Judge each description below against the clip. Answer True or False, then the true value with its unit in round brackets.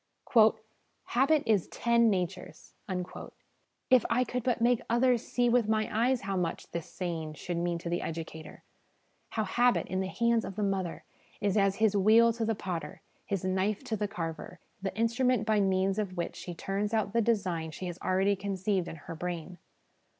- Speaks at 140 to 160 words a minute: False (185 wpm)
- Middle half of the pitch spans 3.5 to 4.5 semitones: True (4.2 semitones)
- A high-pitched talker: True (200 Hz)